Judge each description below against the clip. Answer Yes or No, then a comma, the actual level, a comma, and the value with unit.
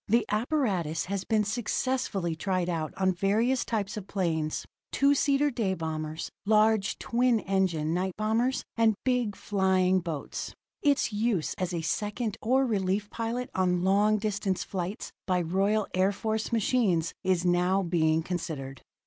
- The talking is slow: No, average, 145 wpm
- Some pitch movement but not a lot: Yes, average, 3.8 semitones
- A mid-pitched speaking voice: No, high, 195 Hz